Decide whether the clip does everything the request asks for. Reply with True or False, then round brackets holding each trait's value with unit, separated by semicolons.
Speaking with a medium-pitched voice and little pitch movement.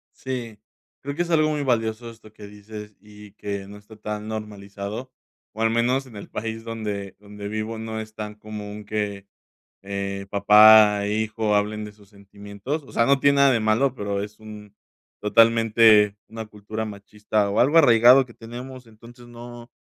False (110 Hz; 2.2 semitones)